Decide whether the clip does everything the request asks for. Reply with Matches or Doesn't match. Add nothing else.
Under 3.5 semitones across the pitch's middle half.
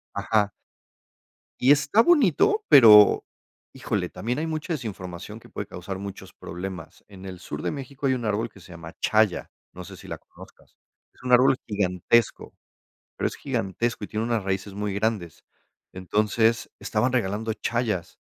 Doesn't match